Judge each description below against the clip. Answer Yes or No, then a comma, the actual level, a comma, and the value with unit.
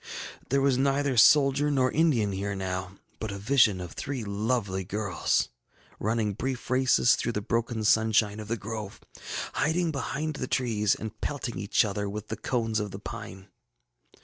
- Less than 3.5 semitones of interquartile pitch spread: No, average, 4.3 semitones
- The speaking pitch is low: Yes, low, 110 Hz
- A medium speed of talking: Yes, average, 165 wpm